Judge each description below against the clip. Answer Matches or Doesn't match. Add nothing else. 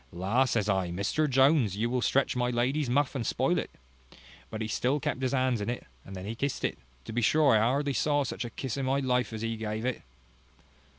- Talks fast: Matches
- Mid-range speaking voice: Doesn't match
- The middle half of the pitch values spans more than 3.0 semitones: Matches